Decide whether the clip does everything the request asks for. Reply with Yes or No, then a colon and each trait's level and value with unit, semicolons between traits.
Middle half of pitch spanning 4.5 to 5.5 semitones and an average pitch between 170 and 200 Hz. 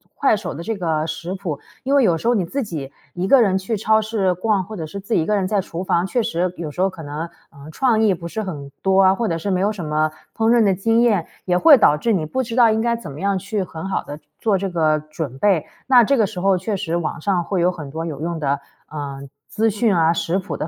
Yes: average, 5.0 semitones; medium, 185 Hz